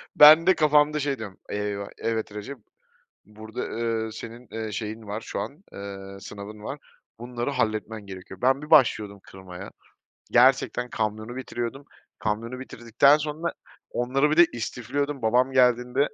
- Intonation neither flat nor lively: Yes, average, 4.3 semitones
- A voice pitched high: No, low, 120 Hz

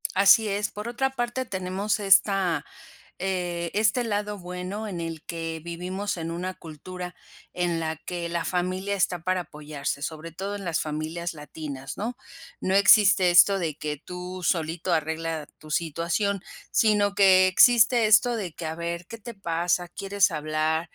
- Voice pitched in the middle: Yes, medium, 180 Hz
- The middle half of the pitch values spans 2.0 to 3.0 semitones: No, average, 3.5 semitones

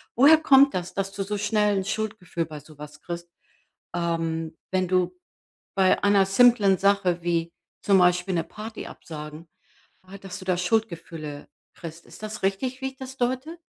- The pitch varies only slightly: No, average, 4.1 semitones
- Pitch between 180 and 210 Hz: Yes, high, 190 Hz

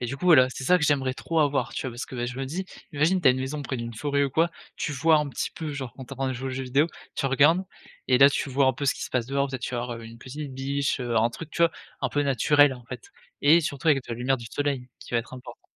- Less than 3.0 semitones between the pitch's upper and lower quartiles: Yes, narrow, 2.5 semitones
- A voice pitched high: No, low, 135 Hz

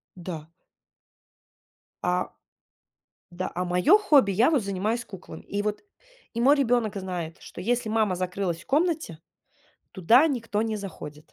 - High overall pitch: Yes, high, 205 Hz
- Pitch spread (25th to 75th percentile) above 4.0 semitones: Yes, average, 5.0 semitones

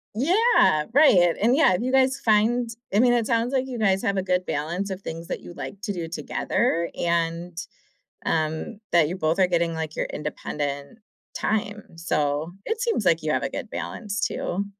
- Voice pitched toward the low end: No, medium, 185 Hz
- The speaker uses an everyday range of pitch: No, wide, 5.8 semitones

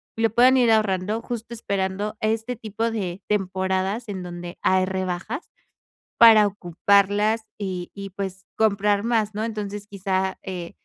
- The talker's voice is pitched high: Yes, high, 205 Hz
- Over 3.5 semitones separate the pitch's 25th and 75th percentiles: No, average, 2.7 semitones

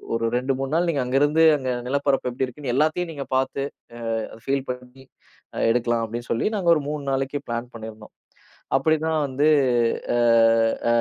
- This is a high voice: No, low, 135 Hz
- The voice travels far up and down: No, average, 3.2 semitones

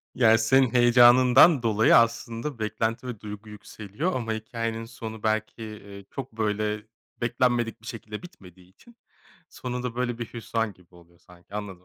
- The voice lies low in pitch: Yes, low, 115 Hz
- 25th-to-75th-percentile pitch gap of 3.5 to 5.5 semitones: No, narrow, 2.5 semitones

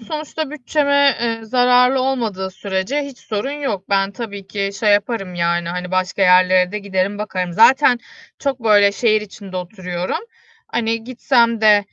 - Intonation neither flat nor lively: Yes, average, 4.7 semitones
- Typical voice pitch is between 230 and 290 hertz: No, high, 210 Hz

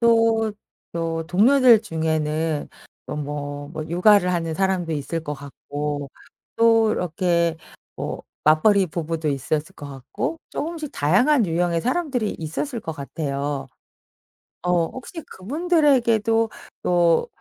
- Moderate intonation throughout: No, wide, 6.7 semitones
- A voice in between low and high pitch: Yes, medium, 170 Hz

